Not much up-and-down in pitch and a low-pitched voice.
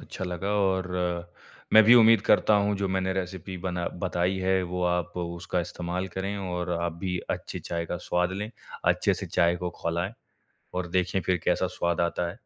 Yes: narrow, 1.5 semitones; very low, 90 Hz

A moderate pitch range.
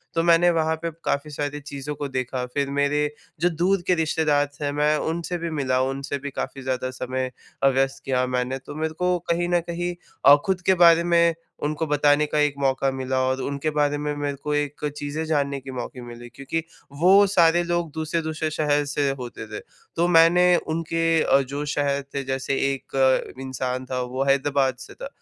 Yes: average, 3.4 semitones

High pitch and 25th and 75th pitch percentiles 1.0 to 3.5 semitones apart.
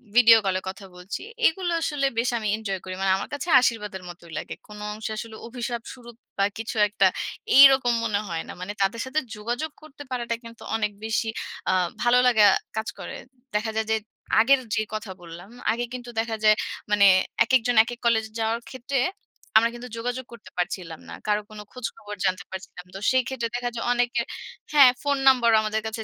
Yes: high, 230 Hz; average, 2.8 semitones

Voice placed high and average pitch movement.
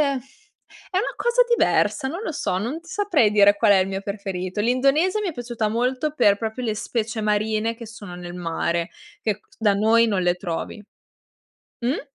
Yes: high, 220 Hz; average, 4.7 semitones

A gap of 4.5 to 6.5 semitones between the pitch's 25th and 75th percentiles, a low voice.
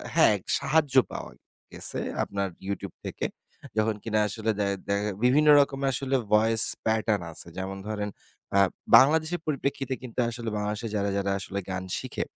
Yes: average, 5.0 semitones; low, 110 Hz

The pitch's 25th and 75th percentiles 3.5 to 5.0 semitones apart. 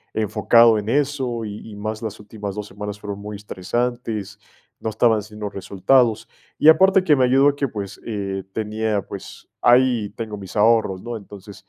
No: average, 2.7 semitones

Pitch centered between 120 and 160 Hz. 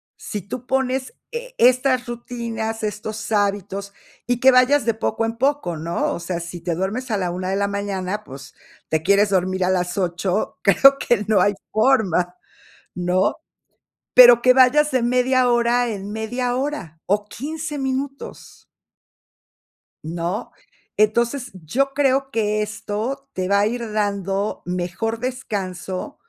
No: high, 215 Hz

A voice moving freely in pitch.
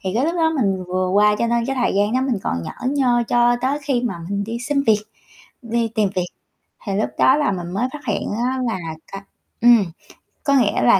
No: average, 4.4 semitones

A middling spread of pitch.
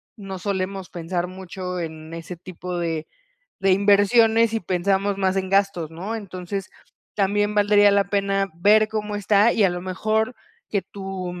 No: narrow, 2.1 semitones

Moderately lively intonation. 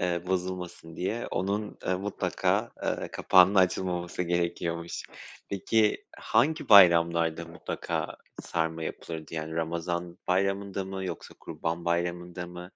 No: narrow, 2.1 semitones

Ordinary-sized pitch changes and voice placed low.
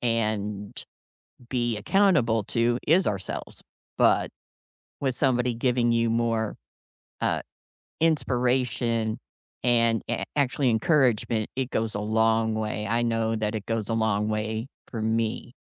No: narrow, 2.0 semitones; low, 115 Hz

